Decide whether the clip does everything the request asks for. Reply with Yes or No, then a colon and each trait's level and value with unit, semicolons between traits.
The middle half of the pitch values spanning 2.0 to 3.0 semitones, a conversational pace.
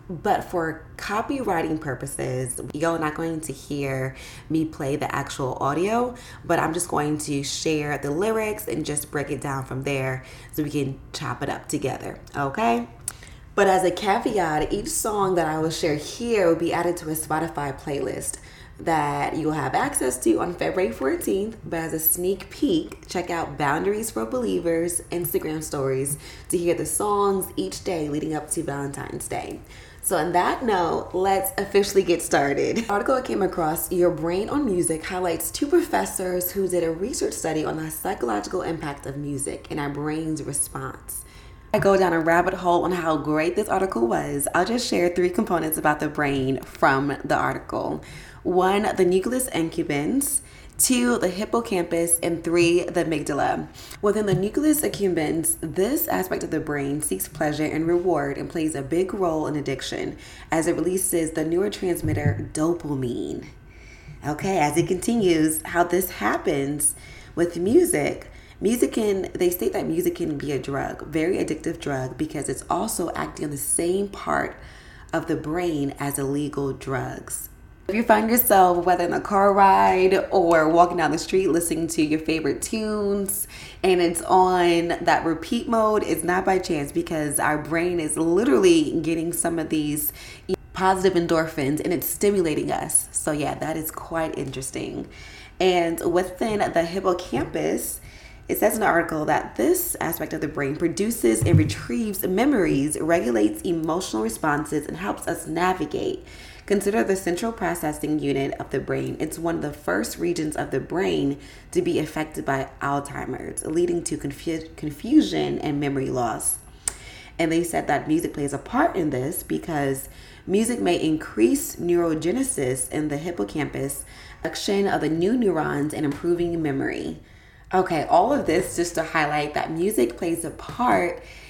No: average, 4.3 semitones; average, 165 wpm